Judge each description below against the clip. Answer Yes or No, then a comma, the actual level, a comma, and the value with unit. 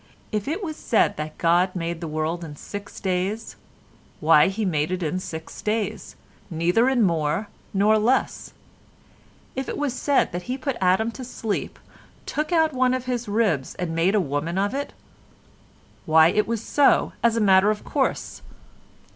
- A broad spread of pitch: Yes, wide, 5.9 semitones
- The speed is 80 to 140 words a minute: No, average, 175 wpm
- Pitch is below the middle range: No, high, 200 Hz